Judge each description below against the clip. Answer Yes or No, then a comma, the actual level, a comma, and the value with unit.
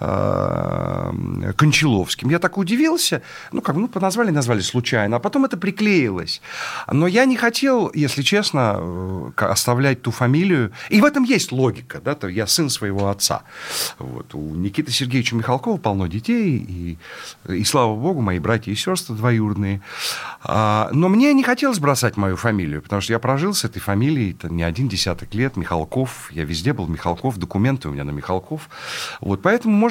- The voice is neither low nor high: No, low, 125 Hz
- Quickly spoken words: Yes, fast, 165 wpm